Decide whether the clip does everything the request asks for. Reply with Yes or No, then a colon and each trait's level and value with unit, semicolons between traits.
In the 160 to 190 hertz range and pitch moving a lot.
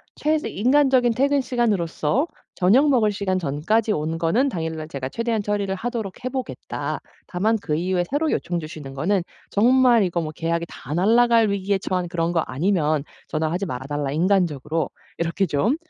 Yes: medium, 185 Hz; wide, 6.1 semitones